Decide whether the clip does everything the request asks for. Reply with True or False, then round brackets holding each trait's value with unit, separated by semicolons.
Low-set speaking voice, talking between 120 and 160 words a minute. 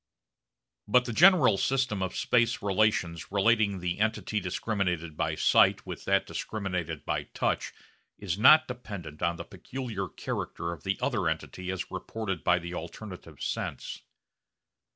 True (100 Hz; 140 wpm)